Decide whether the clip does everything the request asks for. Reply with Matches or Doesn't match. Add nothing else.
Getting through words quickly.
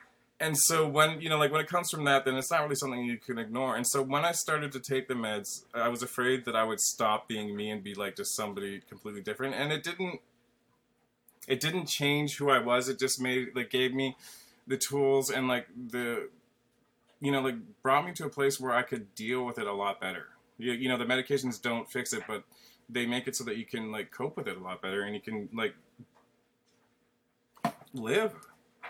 Matches